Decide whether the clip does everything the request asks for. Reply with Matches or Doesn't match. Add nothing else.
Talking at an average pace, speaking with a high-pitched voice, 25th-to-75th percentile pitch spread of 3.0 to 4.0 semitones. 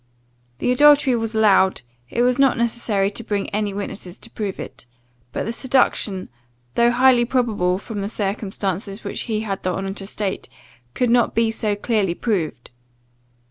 Matches